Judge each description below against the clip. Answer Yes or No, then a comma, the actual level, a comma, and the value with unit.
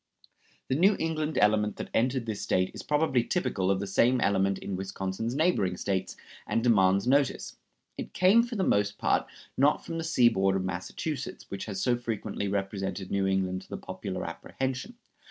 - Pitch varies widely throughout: Yes, wide, 6.2 semitones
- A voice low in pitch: Yes, low, 105 Hz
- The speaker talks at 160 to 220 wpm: Yes, average, 175 wpm